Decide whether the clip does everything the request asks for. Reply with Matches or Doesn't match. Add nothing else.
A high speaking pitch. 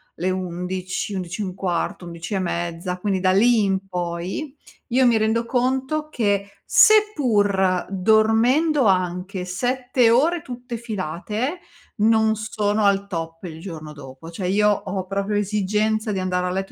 Matches